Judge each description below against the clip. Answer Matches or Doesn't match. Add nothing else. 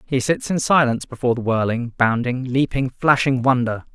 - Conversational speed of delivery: Matches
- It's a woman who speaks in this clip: Doesn't match